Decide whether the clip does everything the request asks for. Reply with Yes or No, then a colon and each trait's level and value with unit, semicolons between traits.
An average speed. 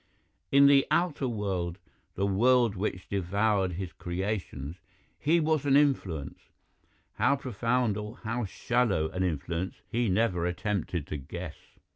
No: slow, 130 wpm